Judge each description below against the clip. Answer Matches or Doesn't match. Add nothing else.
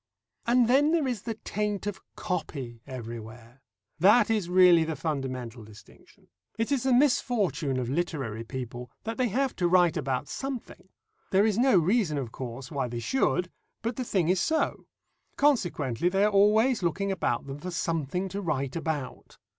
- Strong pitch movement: Matches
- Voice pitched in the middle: Matches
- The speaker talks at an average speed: Matches